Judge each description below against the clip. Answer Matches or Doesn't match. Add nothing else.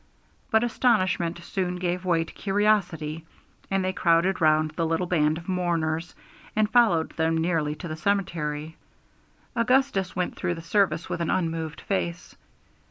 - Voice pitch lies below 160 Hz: Doesn't match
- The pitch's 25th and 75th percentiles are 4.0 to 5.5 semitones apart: Doesn't match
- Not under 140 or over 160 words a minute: Matches